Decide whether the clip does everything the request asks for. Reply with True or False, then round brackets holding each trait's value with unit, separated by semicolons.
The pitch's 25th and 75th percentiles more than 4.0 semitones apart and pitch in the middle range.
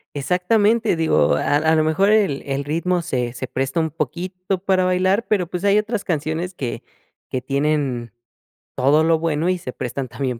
True (4.7 semitones; 160 Hz)